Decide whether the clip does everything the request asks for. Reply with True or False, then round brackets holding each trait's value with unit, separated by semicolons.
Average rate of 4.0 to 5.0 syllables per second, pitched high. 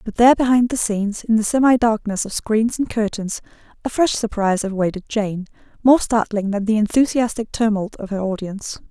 False (5.5 syllables/s; 215 Hz)